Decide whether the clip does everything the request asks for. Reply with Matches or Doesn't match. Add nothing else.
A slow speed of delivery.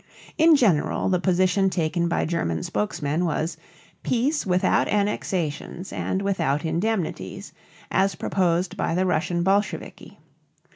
Matches